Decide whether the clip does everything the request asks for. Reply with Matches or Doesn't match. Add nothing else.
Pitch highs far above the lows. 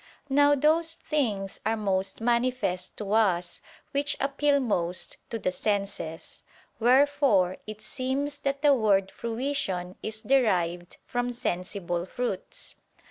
Matches